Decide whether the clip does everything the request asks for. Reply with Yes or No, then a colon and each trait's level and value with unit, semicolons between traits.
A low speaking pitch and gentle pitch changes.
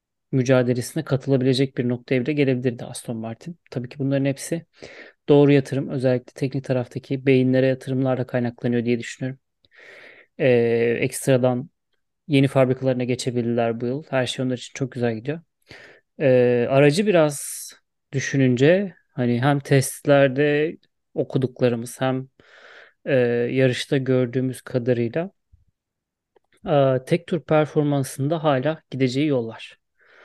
Yes: low, 130 Hz; narrow, 2.2 semitones